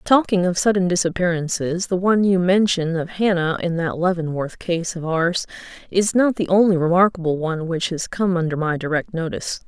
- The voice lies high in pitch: No, medium, 175 Hz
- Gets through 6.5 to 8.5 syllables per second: No, 5.4 syllables/s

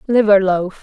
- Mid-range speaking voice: No, high, 200 Hz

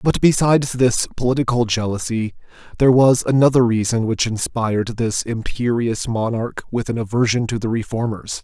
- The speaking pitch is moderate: No, low, 120 Hz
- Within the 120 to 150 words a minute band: Yes, average, 140 wpm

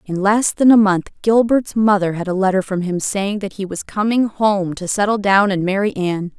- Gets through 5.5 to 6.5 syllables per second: No, 5.1 syllables/s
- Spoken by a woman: Yes, female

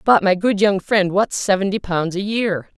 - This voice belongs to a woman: Yes, female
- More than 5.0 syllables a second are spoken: No, 4.6 syllables/s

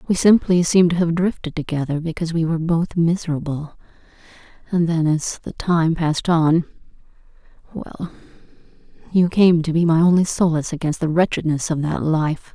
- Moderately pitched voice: Yes, medium, 165 Hz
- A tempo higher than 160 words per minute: No, average, 155 wpm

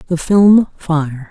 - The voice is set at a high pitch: No, medium, 170 Hz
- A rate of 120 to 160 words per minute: Yes, average, 140 wpm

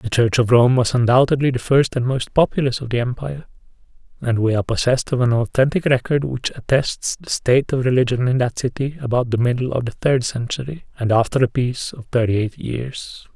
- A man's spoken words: Yes, male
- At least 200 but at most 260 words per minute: Yes, fast, 205 wpm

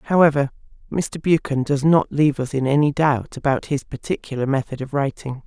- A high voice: No, medium, 140 Hz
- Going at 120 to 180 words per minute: Yes, average, 175 wpm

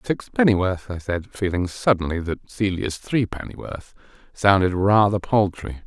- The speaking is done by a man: Yes, male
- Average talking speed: No, slow, 115 wpm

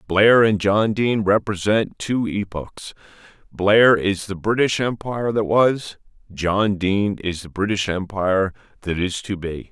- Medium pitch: No, low, 100 Hz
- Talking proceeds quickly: No, average, 150 wpm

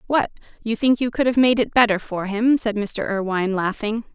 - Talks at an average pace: No, fast, 215 wpm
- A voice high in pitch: Yes, high, 220 Hz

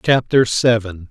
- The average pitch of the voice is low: Yes, low, 110 Hz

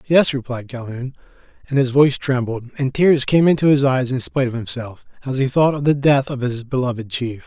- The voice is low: Yes, low, 130 Hz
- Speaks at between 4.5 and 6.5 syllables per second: Yes, 5.6 syllables/s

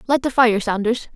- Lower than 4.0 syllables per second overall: No, 5.2 syllables/s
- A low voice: No, high, 235 Hz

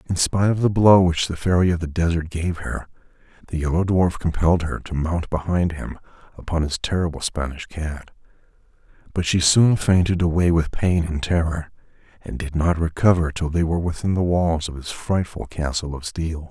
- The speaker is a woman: No, male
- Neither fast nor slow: Yes, average, 190 wpm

